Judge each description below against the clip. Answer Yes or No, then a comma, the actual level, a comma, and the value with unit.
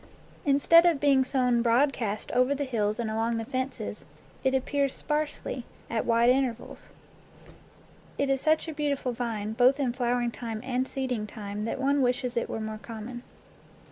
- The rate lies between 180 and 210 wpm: No, average, 165 wpm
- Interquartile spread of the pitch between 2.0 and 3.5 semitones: Yes, average, 3.0 semitones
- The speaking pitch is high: Yes, very high, 250 Hz